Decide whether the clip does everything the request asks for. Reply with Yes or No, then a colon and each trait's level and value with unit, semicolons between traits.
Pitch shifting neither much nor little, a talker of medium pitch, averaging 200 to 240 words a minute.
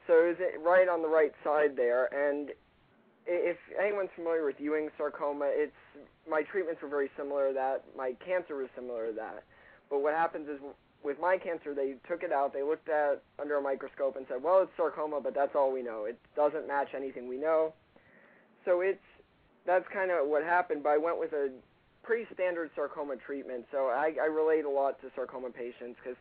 Yes: average, 3.8 semitones; medium, 150 Hz; fast, 205 wpm